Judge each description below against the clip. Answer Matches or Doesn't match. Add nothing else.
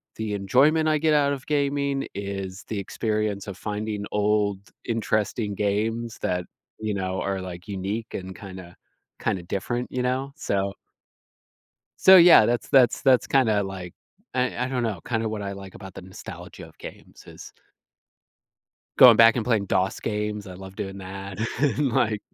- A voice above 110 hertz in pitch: Doesn't match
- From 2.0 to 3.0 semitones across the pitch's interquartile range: Doesn't match